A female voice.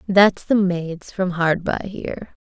Yes: female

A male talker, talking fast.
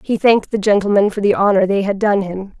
No: female; fast, 255 wpm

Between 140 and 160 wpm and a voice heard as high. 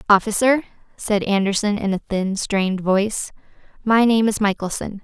Yes: average, 145 wpm; high, 205 Hz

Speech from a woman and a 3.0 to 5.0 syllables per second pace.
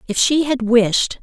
Yes: female; 4.9 syllables/s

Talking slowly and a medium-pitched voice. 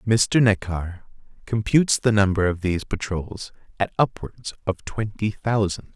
No: slow, 130 wpm; low, 105 Hz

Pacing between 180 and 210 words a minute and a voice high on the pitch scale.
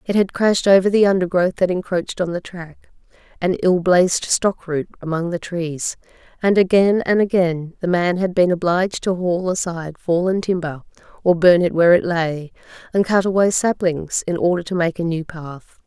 No: average, 190 wpm; medium, 175 Hz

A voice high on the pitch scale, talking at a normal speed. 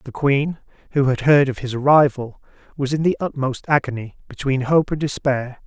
No: low, 135 Hz; average, 180 wpm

